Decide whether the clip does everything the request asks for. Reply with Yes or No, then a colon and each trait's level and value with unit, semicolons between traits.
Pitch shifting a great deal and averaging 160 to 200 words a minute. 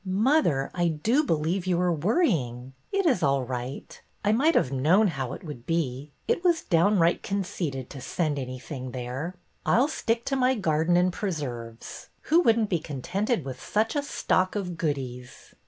Yes: wide, 8.0 semitones; average, 180 wpm